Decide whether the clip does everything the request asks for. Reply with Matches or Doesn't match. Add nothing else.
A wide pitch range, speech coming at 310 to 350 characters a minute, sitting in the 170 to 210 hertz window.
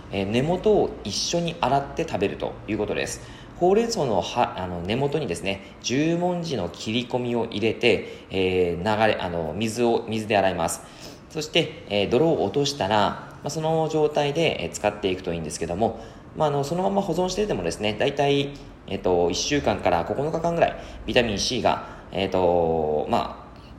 Doesn't match